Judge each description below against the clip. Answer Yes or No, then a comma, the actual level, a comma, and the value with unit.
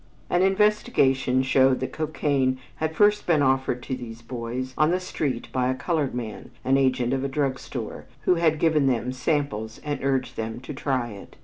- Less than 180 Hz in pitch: Yes, low, 135 Hz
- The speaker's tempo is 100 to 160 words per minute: No, average, 190 wpm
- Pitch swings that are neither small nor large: Yes, average, 3.3 semitones